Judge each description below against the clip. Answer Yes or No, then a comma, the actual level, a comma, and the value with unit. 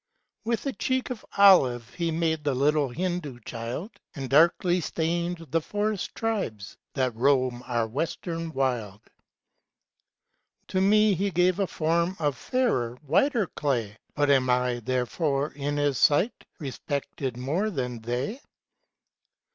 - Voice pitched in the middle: Yes, medium, 150 Hz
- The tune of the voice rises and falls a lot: Yes, wide, 6.0 semitones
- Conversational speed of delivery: No, slow, 130 wpm